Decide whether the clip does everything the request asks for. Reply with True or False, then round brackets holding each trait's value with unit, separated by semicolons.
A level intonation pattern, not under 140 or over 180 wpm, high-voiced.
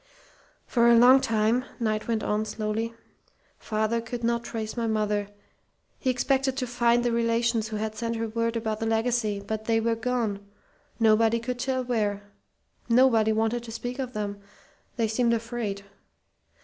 True (1.8 semitones; 160 wpm; 230 Hz)